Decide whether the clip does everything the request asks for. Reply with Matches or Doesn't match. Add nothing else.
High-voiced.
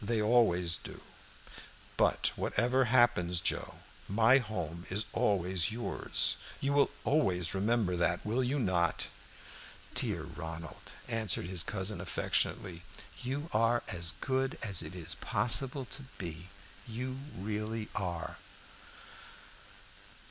Doesn't match